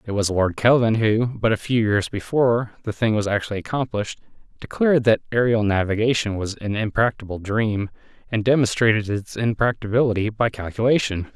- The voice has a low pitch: Yes, low, 110 Hz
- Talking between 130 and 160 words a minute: Yes, average, 155 wpm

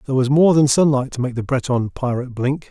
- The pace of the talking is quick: Yes, fast, 245 wpm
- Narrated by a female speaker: No, male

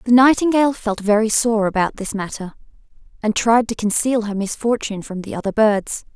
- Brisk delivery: No, average, 175 wpm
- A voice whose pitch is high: Yes, high, 220 Hz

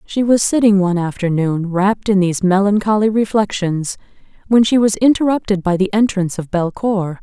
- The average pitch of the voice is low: No, high, 200 Hz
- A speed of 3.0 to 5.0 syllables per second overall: No, 5.5 syllables/s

